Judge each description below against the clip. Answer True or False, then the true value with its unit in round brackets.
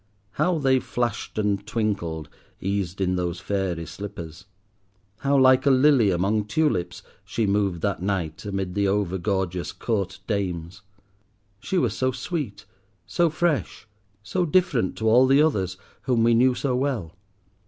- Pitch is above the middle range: False (105 Hz)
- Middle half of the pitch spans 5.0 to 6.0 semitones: True (5.6 semitones)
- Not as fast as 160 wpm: True (145 wpm)